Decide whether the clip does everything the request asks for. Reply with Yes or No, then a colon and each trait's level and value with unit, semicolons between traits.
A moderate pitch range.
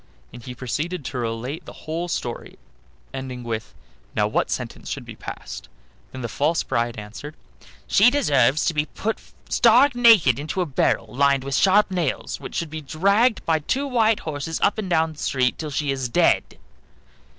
No: wide, 6.4 semitones